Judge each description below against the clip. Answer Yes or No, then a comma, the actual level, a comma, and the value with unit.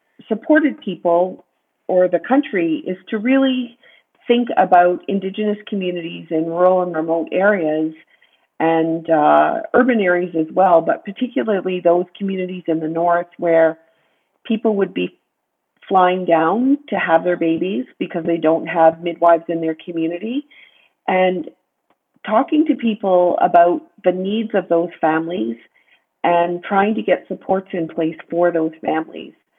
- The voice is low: No, medium, 180 Hz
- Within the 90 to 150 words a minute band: Yes, average, 140 wpm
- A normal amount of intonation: Yes, average, 4.0 semitones